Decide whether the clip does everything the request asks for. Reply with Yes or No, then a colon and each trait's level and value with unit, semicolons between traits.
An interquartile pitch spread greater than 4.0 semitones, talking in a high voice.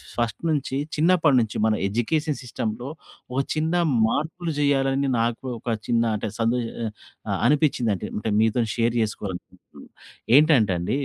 No: average, 4.7 semitones; low, 125 Hz